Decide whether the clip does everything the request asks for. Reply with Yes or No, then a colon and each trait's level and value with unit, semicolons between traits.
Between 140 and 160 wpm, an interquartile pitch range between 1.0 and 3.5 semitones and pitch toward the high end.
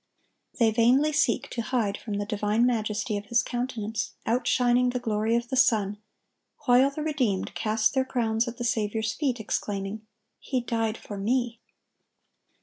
Yes: average, 155 wpm; narrow, 2.6 semitones; high, 230 Hz